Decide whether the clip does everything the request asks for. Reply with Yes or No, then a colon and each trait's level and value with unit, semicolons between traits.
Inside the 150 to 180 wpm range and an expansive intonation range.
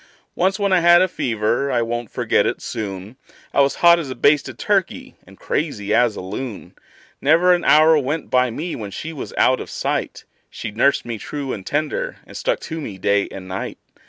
No: fast, 205 wpm; wide, 6.8 semitones